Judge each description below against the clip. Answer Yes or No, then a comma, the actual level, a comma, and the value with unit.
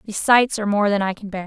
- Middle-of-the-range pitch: No, high, 205 Hz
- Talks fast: Yes, fast, 330 wpm